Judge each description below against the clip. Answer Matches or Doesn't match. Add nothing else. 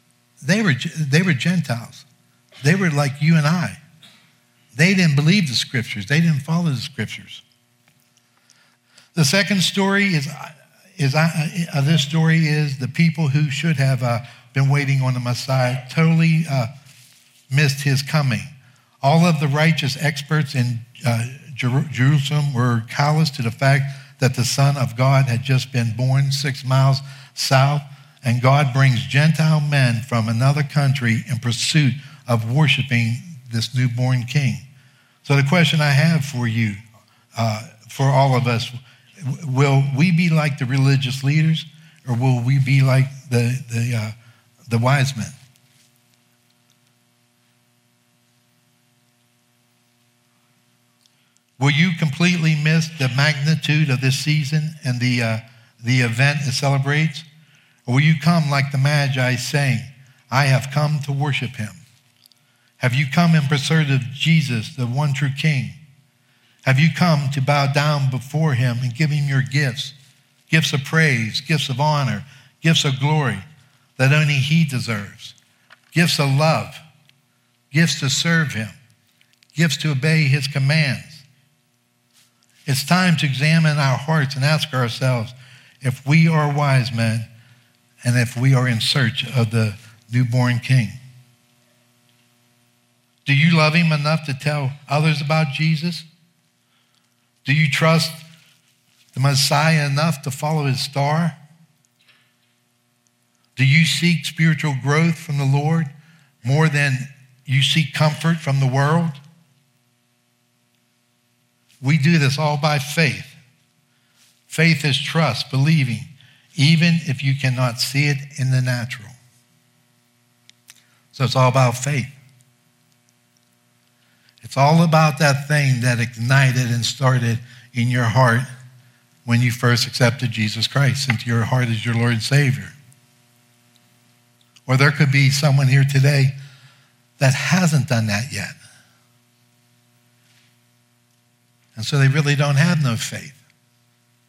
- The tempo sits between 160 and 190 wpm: Doesn't match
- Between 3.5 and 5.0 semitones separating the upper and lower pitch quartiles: Matches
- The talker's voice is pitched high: Doesn't match